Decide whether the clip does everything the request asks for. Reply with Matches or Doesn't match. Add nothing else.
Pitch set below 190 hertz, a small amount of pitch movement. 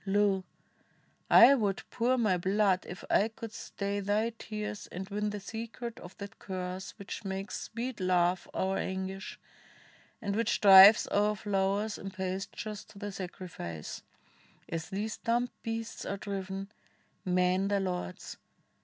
Doesn't match